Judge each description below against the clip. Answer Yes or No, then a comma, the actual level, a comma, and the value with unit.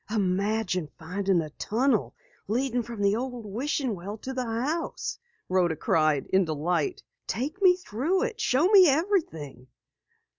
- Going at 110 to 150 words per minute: Yes, average, 140 wpm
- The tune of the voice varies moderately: No, wide, 7.4 semitones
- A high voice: Yes, high, 225 Hz